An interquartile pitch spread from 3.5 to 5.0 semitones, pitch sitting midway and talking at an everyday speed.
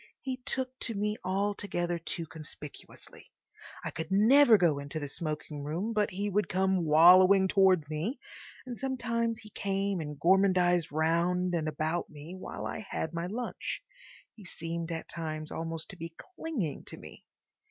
Yes: average, 4.2 semitones; medium, 180 Hz; average, 160 wpm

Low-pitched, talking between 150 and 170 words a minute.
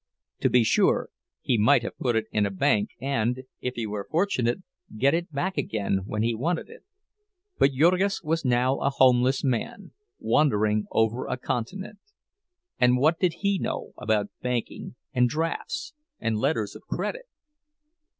Yes: low, 125 Hz; average, 160 wpm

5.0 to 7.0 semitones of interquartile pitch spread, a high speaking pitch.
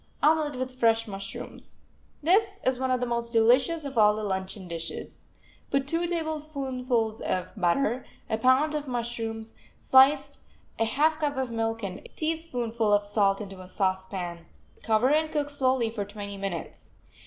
Yes: wide, 5.4 semitones; high, 235 Hz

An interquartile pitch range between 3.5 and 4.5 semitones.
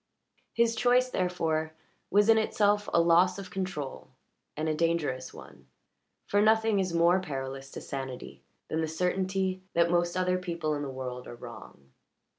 Yes: average, 4.0 semitones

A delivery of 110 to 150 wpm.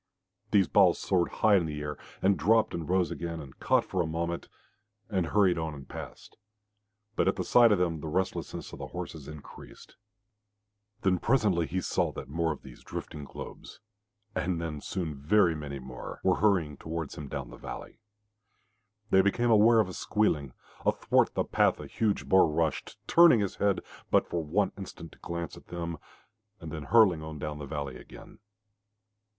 No: average, 180 wpm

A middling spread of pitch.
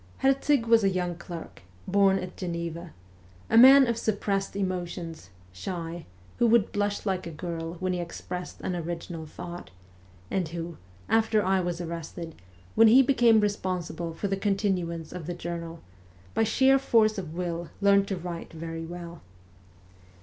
Yes: average, 3.3 semitones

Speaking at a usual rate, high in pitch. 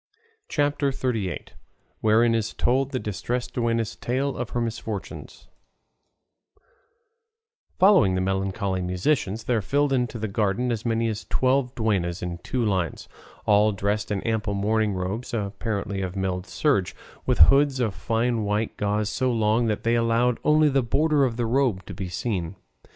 No: average, 155 wpm; low, 110 Hz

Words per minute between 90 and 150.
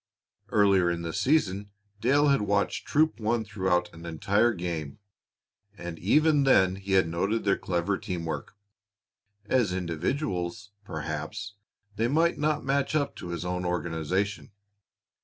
Yes: average, 140 wpm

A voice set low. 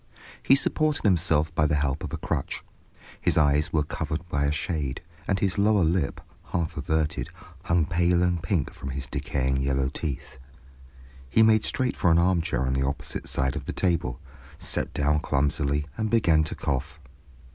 Yes: very low, 80 Hz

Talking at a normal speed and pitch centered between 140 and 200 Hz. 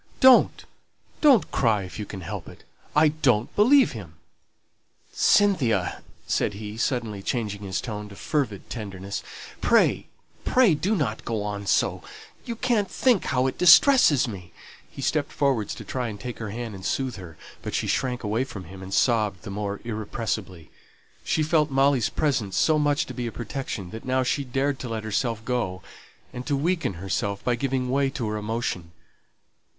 No: average, 175 wpm; low, 120 Hz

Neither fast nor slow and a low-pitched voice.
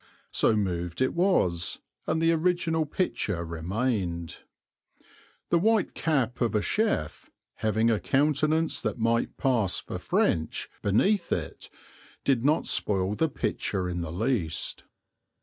No: slow, 130 wpm; low, 115 Hz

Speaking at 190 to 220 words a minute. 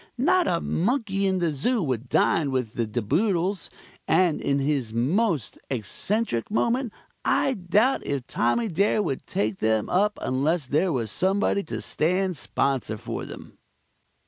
No: average, 150 wpm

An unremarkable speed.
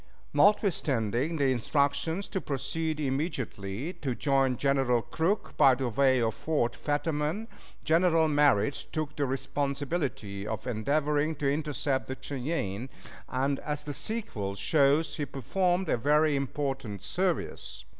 No: slow, 125 wpm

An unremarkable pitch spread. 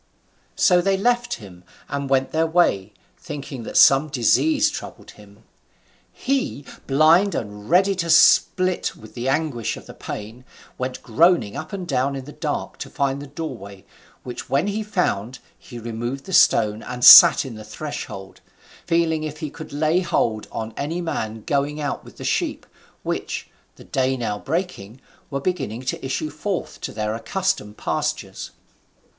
No: wide, 6.3 semitones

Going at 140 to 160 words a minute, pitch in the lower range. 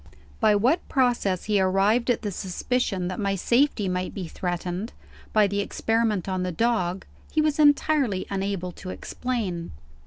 No: average, 155 wpm; high, 200 Hz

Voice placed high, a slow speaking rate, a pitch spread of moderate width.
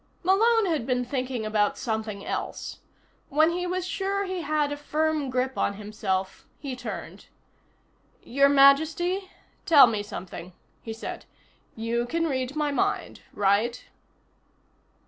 No: very high, 275 Hz; slow, 130 wpm; wide, 6.5 semitones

